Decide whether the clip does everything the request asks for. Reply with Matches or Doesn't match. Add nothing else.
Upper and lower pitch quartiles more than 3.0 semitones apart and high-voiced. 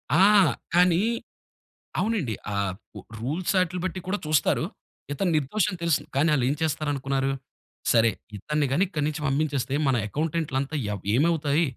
Doesn't match